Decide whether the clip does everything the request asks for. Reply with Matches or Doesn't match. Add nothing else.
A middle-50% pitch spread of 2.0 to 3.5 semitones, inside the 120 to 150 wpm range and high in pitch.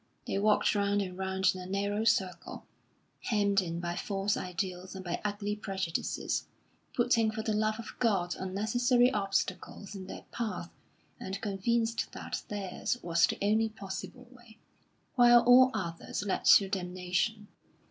Matches